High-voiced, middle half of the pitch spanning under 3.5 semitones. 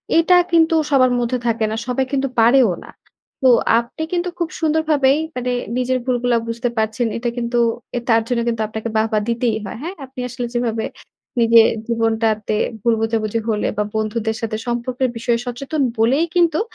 Yes: high, 240 Hz; average, 2.8 semitones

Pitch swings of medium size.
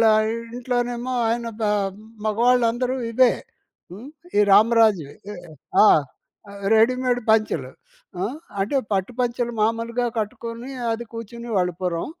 No: narrow, 2.2 semitones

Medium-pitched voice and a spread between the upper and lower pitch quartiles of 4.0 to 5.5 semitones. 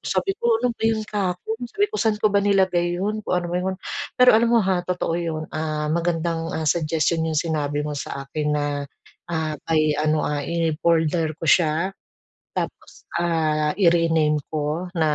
No: medium, 165 Hz; average, 3.3 semitones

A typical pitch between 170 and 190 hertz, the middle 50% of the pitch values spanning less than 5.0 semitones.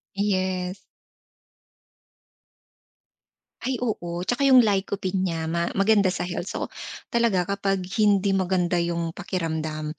Yes: medium, 185 Hz; average, 2.7 semitones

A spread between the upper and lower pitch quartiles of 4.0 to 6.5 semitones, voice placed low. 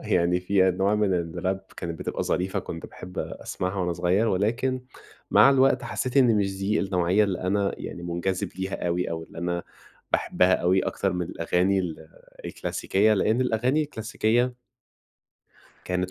No: average, 3.3 semitones; very low, 95 Hz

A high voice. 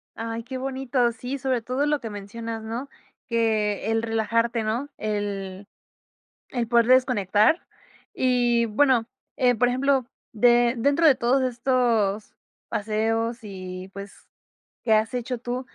Yes: high, 235 Hz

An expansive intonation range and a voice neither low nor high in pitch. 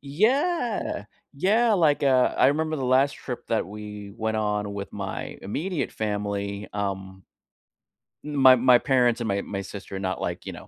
No: wide, 6.0 semitones; low, 120 Hz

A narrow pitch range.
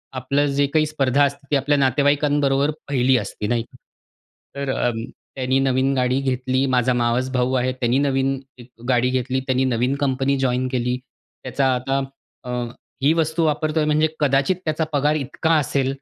Yes: narrow, 2.0 semitones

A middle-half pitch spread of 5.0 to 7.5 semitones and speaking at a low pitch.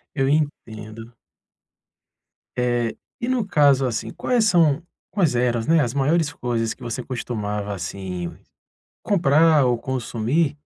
Yes: average, 5.3 semitones; low, 130 Hz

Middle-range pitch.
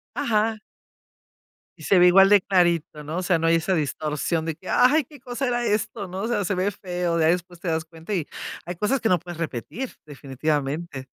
Yes: medium, 180 Hz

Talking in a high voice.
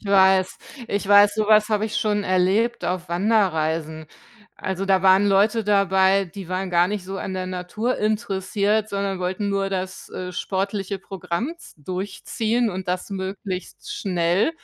Yes: high, 195 Hz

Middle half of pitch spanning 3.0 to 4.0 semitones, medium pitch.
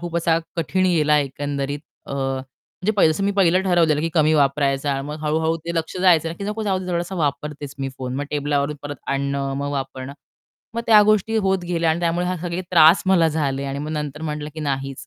Yes: average, 3.7 semitones; medium, 155 Hz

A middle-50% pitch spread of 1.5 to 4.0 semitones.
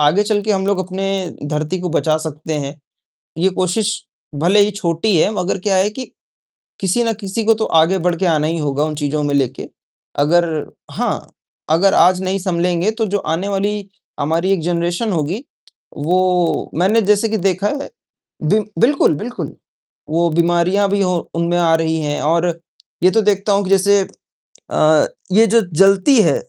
Yes: average, 3.7 semitones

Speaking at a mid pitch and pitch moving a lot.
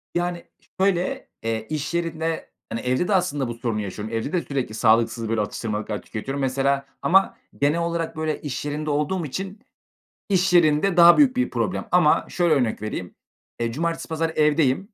Yes: medium, 150 Hz; wide, 6.4 semitones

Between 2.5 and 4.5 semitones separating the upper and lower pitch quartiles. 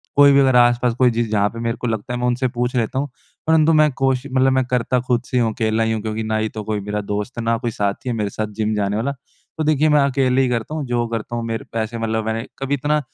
Yes: average, 2.9 semitones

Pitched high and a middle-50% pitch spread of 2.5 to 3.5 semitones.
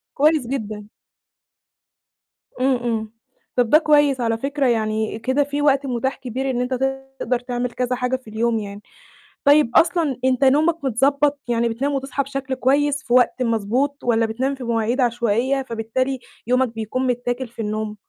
Yes: very high, 255 Hz; average, 3.0 semitones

